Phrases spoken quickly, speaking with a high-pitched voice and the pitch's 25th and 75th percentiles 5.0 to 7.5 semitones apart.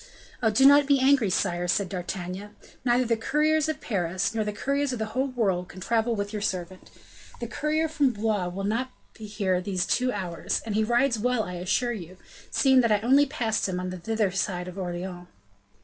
Yes: fast, 210 wpm; high, 215 Hz; average, 5.3 semitones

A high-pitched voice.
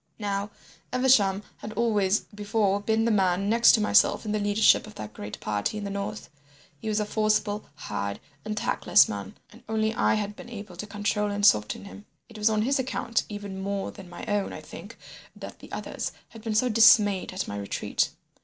Yes: high, 210 Hz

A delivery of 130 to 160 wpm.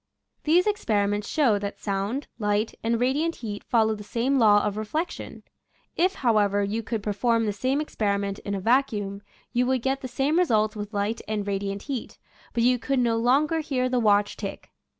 No: average, 190 wpm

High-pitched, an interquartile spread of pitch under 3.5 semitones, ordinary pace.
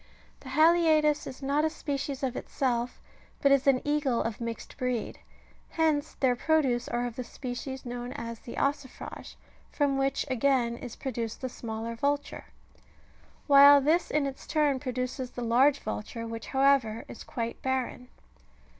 Yes: very high, 260 Hz; average, 3.0 semitones; average, 160 wpm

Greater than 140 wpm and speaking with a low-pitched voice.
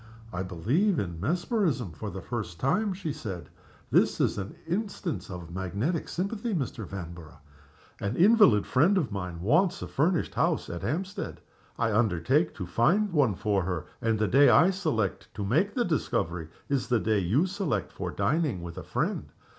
Yes: average, 170 wpm; low, 120 Hz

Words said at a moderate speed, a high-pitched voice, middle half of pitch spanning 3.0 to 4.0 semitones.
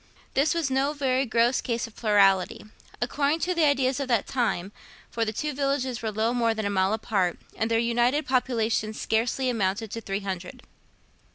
Yes: average, 185 wpm; high, 235 Hz; average, 3.6 semitones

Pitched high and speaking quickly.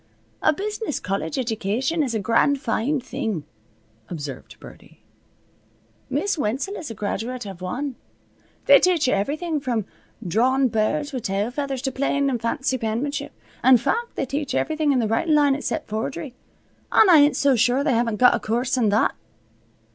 No: very high, 255 Hz; average, 170 wpm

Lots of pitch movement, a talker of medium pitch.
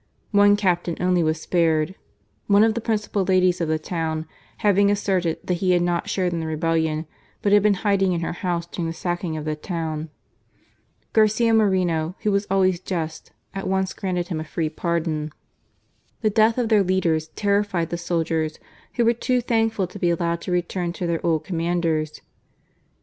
No: average, 3.5 semitones; medium, 175 Hz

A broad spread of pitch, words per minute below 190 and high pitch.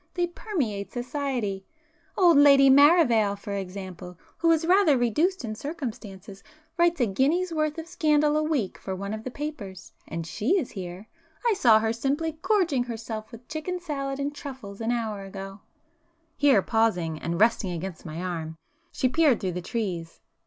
Yes: wide, 7.6 semitones; average, 165 wpm; high, 240 Hz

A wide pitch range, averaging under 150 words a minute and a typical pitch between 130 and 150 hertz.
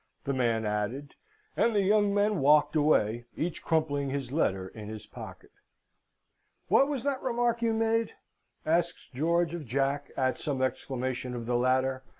No: wide, 7.4 semitones; average, 155 wpm; medium, 140 Hz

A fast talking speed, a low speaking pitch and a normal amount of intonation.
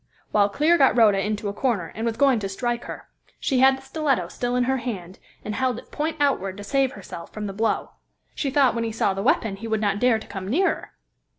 No: fast, 240 wpm; high, 230 Hz; average, 4.6 semitones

